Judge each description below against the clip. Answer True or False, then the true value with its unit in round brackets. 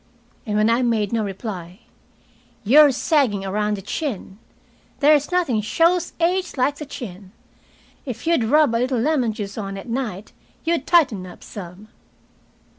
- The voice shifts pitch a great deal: True (6.4 semitones)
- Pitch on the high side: True (230 Hz)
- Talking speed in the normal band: True (150 wpm)